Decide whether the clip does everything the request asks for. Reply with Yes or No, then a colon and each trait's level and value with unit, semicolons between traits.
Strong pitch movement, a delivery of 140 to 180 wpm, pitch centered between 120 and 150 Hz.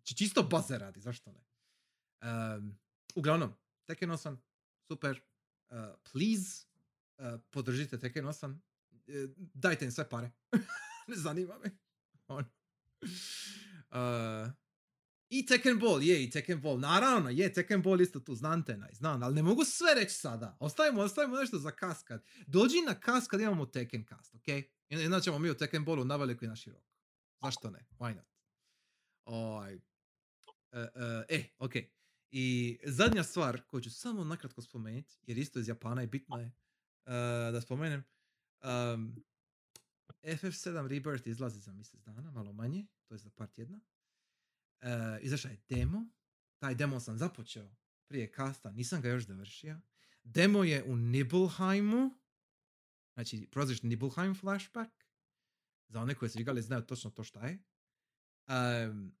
Yes: wide, 7.1 semitones; average, 155 wpm; low, 135 Hz